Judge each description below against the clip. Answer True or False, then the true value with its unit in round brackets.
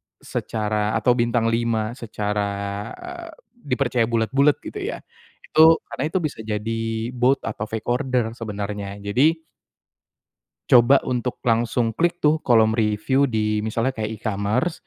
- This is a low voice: True (115 Hz)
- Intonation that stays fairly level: False (3.5 semitones)